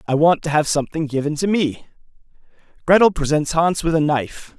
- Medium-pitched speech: Yes, medium, 155 Hz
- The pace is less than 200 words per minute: Yes, average, 185 wpm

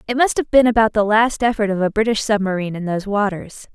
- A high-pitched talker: Yes, high, 210 Hz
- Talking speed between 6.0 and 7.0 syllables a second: Yes, 6.5 syllables/s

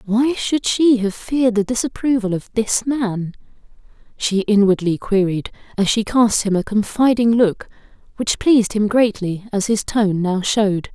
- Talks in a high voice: Yes, high, 220 Hz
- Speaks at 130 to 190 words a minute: Yes, average, 160 wpm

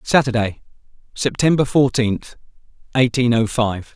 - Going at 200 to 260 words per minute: No, slow, 90 wpm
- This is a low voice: Yes, low, 120 Hz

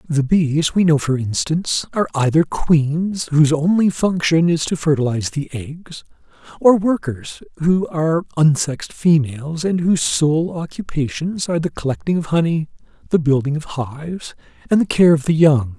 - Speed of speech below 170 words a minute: Yes, average, 160 wpm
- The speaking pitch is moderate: Yes, medium, 155 Hz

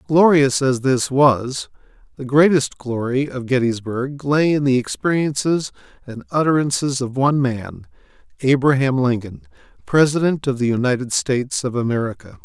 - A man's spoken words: Yes, male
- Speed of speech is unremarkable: No, slow, 130 wpm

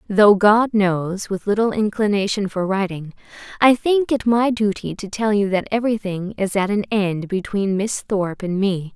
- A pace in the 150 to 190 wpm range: Yes, average, 180 wpm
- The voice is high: Yes, high, 205 Hz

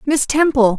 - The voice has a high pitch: Yes, very high, 260 Hz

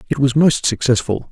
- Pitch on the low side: Yes, low, 130 Hz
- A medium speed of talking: Yes, average, 180 wpm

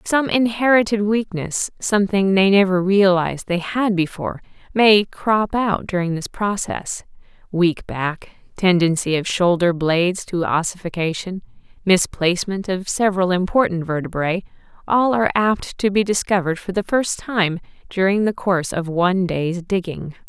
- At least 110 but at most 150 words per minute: Yes, slow, 135 wpm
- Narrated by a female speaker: Yes, female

